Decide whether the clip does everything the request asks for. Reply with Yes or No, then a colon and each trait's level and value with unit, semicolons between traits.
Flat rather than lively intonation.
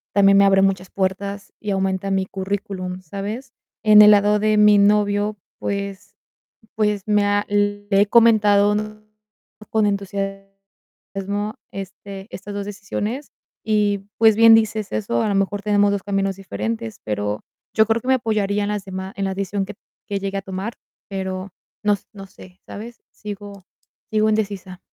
Yes: narrow, 1.3 semitones